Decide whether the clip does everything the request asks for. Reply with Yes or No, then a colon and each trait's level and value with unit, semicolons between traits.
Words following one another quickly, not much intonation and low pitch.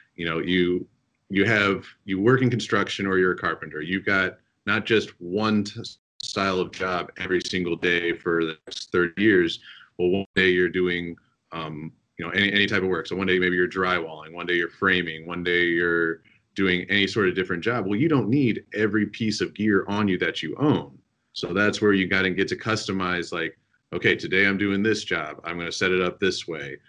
Yes: fast, 220 wpm; narrow, 2.3 semitones; very low, 95 Hz